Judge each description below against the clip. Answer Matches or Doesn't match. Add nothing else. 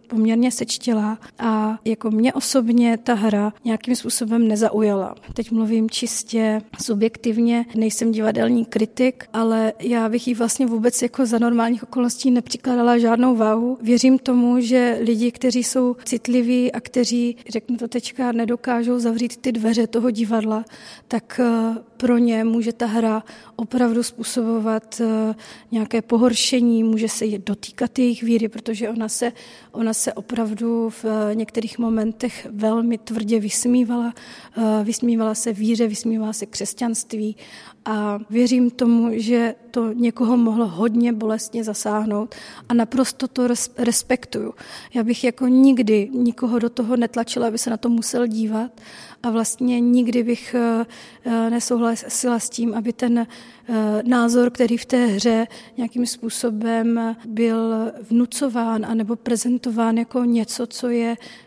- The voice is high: Matches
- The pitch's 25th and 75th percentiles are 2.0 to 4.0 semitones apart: Doesn't match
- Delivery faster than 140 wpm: Doesn't match